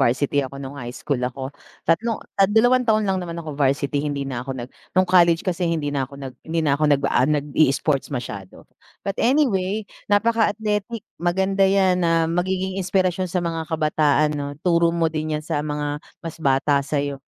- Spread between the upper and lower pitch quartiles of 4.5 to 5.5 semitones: Yes, average, 4.8 semitones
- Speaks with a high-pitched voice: No, medium, 160 Hz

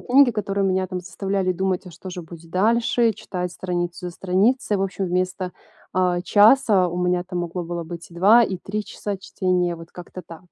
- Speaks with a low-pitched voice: No, medium, 185 Hz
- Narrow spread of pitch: Yes, narrow, 2.1 semitones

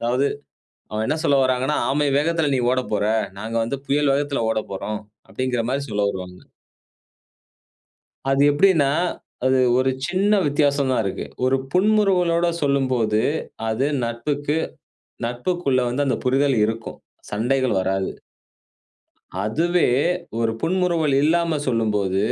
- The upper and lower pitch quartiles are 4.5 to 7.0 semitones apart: Yes, average, 4.8 semitones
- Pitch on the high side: No, low, 135 Hz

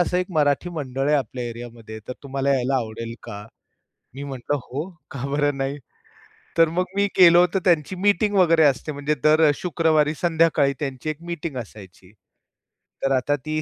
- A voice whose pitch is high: No, medium, 145 Hz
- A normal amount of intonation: Yes, average, 4.0 semitones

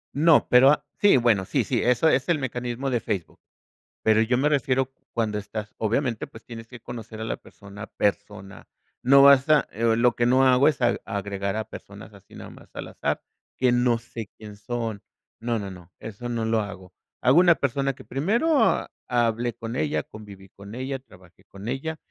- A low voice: Yes, low, 120 Hz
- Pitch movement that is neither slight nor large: Yes, average, 3.7 semitones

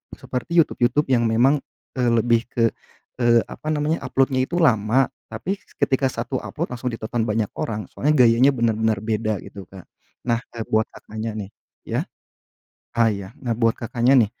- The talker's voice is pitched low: Yes, low, 115 Hz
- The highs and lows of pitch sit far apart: No, average, 2.9 semitones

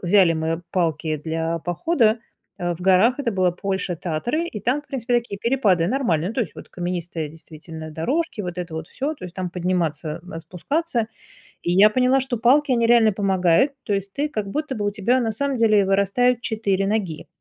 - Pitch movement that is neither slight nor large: No, wide, 5.8 semitones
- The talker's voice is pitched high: Yes, high, 195 Hz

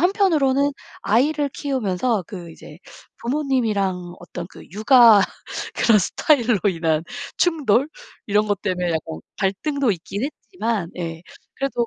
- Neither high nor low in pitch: No, high, 220 Hz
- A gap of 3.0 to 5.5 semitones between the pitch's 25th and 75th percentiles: No, wide, 7.2 semitones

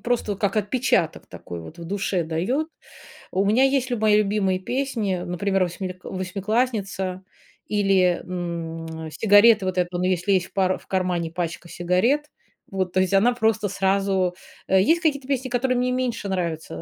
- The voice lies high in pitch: Yes, high, 195 Hz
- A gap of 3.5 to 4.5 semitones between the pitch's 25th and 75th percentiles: Yes, average, 3.8 semitones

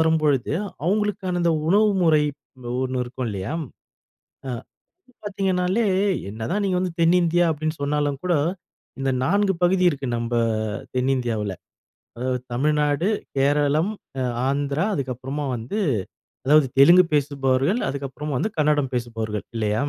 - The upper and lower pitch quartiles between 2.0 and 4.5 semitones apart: No, average, 5.1 semitones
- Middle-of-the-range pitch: Yes, medium, 145 Hz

